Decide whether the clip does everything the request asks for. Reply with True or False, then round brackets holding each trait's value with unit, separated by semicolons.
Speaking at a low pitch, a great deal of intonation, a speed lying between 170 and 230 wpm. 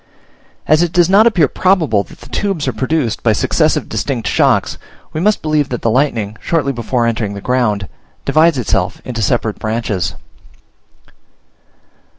False (125 Hz; 6.4 semitones; 155 wpm)